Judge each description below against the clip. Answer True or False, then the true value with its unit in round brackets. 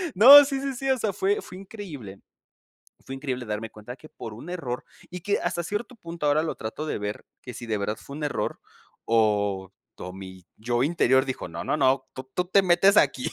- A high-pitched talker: False (140 Hz)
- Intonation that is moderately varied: False (8.8 semitones)